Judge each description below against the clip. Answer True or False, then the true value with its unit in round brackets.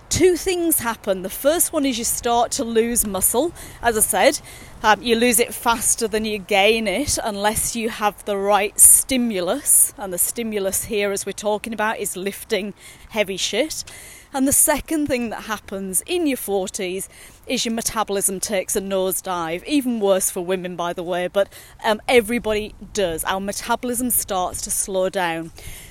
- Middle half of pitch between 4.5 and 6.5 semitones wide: False (3.7 semitones)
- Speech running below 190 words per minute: True (170 wpm)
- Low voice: False (210 Hz)